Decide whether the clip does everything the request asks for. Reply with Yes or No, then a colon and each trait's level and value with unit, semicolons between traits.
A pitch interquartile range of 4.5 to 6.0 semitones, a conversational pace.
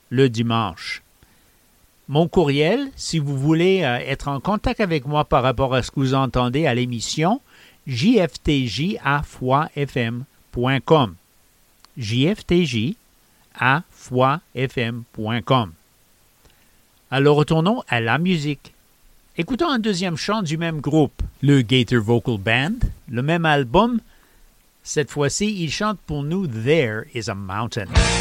No: average, 5.1 semitones; slow, 115 wpm